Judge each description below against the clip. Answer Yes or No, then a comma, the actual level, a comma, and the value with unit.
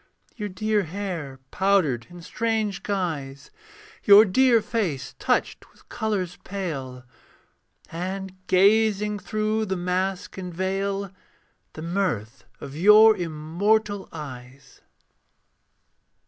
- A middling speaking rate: No, slow, 100 wpm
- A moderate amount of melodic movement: Yes, average, 4.4 semitones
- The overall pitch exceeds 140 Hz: Yes, high, 190 Hz